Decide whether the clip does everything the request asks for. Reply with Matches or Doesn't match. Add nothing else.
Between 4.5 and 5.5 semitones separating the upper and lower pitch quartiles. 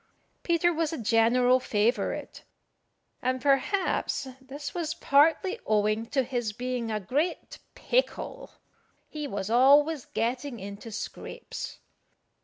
Matches